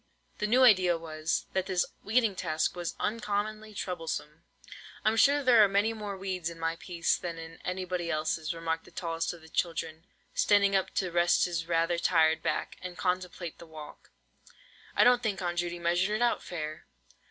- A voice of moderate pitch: Yes, medium, 175 Hz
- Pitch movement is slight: No, average, 3.4 semitones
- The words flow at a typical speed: Yes, average, 180 wpm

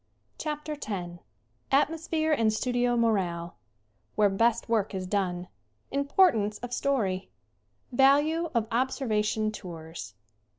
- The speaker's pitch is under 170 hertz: No, high, 225 Hz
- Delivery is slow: Yes, slow, 100 wpm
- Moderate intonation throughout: No, wide, 6.1 semitones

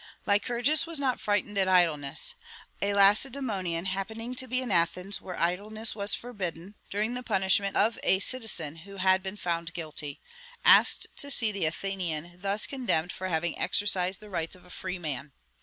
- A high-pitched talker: Yes, high, 195 Hz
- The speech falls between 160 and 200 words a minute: Yes, average, 170 wpm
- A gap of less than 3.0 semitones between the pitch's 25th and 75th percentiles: No, average, 3.9 semitones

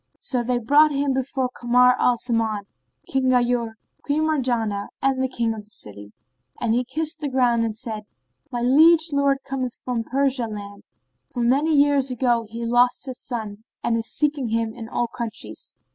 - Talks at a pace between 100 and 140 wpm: No, average, 180 wpm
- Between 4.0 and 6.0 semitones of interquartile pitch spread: No, average, 3.0 semitones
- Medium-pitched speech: No, high, 245 Hz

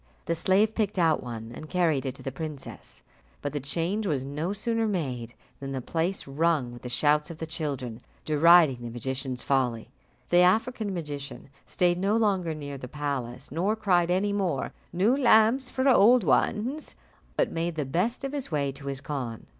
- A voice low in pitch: No, medium, 160 Hz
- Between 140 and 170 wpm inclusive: No, average, 185 wpm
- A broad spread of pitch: Yes, wide, 6.3 semitones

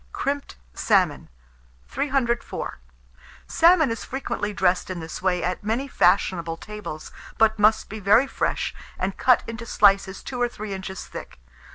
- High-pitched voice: Yes, high, 210 Hz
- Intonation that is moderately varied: Yes, average, 4.2 semitones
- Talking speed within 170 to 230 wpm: No, average, 145 wpm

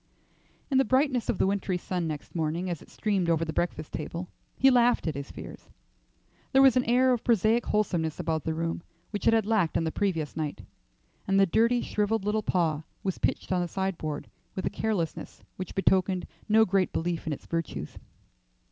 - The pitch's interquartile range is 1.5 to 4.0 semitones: No, average, 4.9 semitones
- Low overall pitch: No, medium, 185 Hz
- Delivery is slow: No, average, 200 wpm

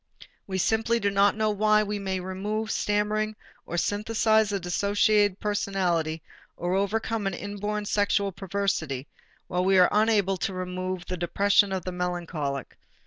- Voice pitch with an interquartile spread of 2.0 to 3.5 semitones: Yes, narrow, 2.4 semitones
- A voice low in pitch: No, high, 200 Hz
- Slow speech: No, average, 145 wpm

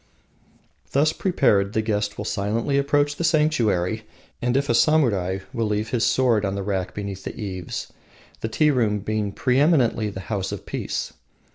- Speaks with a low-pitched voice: Yes, low, 110 Hz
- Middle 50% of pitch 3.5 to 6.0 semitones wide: Yes, wide, 5.5 semitones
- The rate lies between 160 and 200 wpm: Yes, average, 165 wpm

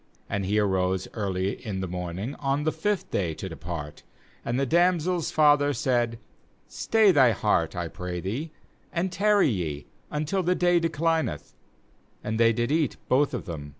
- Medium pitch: No, low, 125 Hz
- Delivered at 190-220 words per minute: No, average, 170 wpm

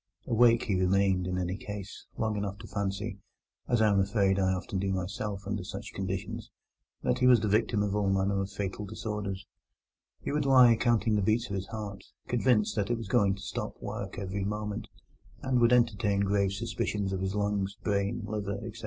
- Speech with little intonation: Yes, narrow, 2.1 semitones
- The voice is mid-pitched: No, low, 100 Hz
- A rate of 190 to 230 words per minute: Yes, average, 195 wpm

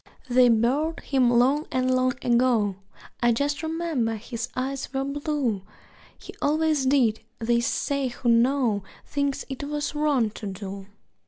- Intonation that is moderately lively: Yes, average, 3.5 semitones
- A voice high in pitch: Yes, very high, 255 Hz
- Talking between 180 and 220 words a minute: No, average, 145 wpm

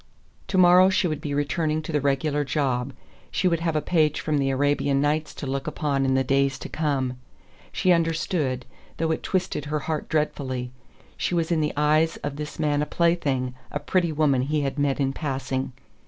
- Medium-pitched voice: Yes, medium, 150 Hz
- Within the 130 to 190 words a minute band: No, average, 200 wpm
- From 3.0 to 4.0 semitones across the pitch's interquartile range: No, narrow, 2.6 semitones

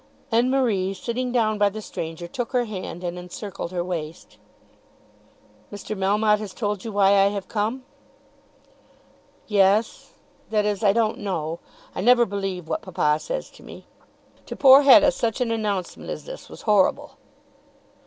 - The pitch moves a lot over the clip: No, average, 3.5 semitones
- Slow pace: No, average, 155 wpm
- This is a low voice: No, high, 205 Hz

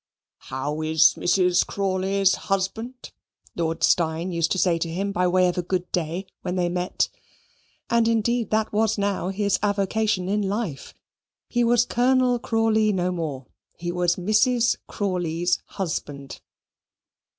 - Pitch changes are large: No, average, 3.7 semitones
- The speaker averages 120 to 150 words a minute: Yes, average, 140 wpm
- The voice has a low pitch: No, high, 190 Hz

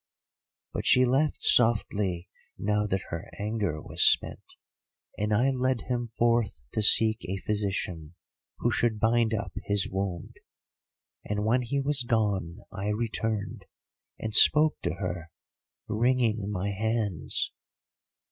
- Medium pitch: No, low, 105 Hz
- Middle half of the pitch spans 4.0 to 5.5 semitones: No, average, 3.2 semitones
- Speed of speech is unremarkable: No, slow, 130 wpm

